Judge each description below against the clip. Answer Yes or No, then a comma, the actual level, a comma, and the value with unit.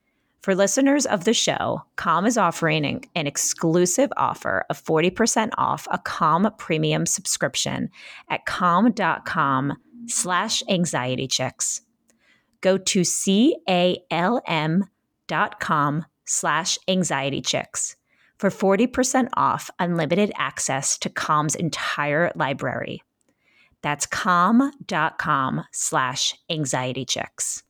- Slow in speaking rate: Yes, slow, 95 wpm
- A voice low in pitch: No, medium, 180 Hz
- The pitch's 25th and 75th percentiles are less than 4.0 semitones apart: No, average, 5.3 semitones